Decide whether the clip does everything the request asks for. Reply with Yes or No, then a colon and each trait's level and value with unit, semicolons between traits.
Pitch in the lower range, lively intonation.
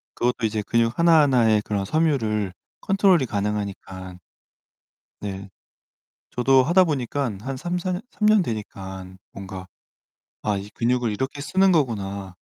Yes: low, 115 Hz; wide, 6.6 semitones